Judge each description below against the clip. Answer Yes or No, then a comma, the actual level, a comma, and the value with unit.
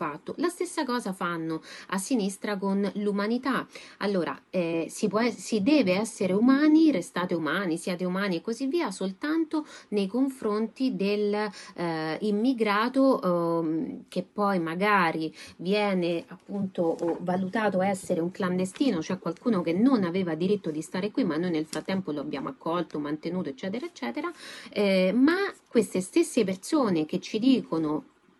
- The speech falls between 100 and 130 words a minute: No, average, 140 wpm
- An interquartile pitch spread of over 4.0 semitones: Yes, wide, 5.4 semitones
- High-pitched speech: Yes, high, 200 Hz